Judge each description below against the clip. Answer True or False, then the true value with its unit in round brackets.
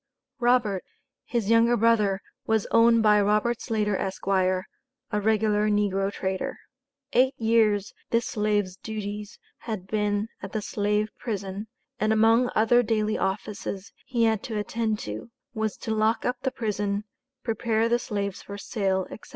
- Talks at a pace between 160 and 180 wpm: False (145 wpm)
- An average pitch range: False (2.0 semitones)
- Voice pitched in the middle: False (215 Hz)